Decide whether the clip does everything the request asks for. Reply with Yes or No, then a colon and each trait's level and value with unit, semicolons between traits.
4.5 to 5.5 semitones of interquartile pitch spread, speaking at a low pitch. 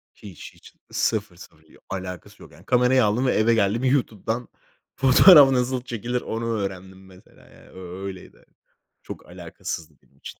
Yes: average, 4.9 semitones; low, 110 Hz